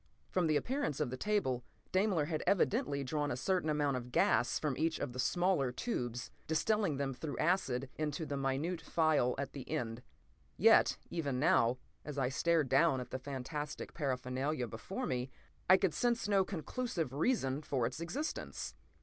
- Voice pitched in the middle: Yes, medium, 145 Hz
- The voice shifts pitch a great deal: No, average, 5.0 semitones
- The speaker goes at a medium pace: Yes, average, 170 wpm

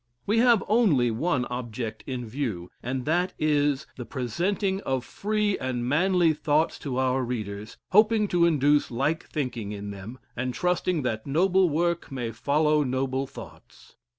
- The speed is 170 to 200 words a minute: No, average, 155 wpm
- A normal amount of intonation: No, wide, 6.0 semitones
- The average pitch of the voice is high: No, medium, 140 Hz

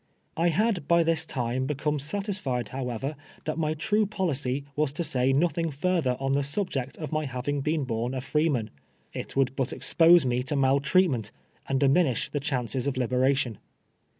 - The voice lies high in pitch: No, medium, 140 Hz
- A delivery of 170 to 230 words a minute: Yes, average, 175 wpm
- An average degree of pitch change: Yes, average, 3.8 semitones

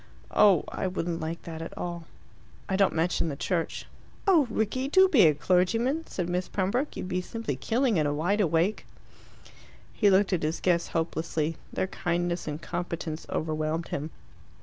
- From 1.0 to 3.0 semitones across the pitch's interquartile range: No, average, 4.0 semitones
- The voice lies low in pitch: No, medium, 175 Hz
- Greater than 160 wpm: Yes, average, 170 wpm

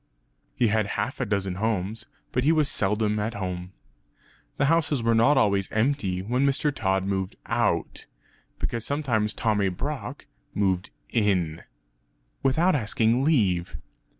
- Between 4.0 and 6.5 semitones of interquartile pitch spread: Yes, average, 5.2 semitones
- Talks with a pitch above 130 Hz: No, low, 110 Hz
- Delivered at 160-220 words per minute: No, slow, 135 wpm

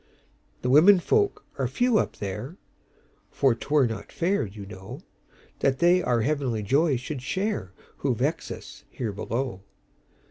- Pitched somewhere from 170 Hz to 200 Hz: No, low, 135 Hz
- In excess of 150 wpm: No, slow, 135 wpm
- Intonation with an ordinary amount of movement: No, wide, 7.6 semitones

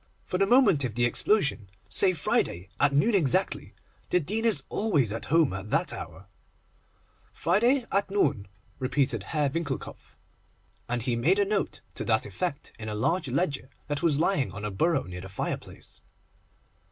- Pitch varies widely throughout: Yes, wide, 8.2 semitones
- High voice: No, medium, 145 Hz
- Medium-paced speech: Yes, average, 165 wpm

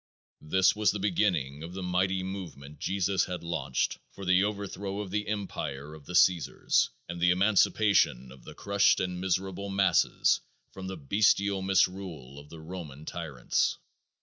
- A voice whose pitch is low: Yes, very low, 90 Hz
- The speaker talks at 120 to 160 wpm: Yes, average, 155 wpm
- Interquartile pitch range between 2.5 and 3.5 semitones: No, average, 3.9 semitones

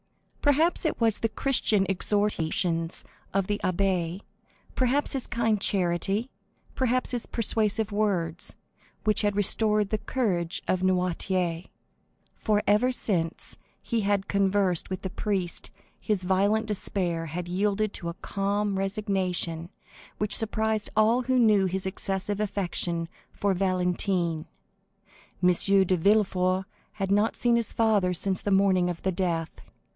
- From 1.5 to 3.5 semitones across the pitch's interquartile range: Yes, average, 2.9 semitones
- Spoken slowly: Yes, slow, 130 wpm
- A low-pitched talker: No, high, 195 Hz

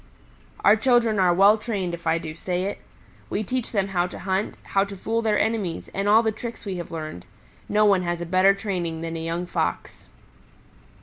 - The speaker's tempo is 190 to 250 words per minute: Yes, fast, 205 wpm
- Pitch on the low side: No, high, 195 Hz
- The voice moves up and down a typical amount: Yes, average, 3.6 semitones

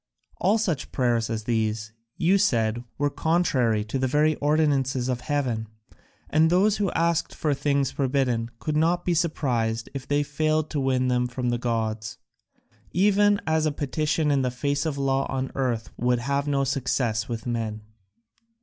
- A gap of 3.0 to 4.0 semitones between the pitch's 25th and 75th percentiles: No, average, 4.4 semitones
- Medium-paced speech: Yes, average, 170 wpm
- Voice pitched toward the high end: No, low, 135 Hz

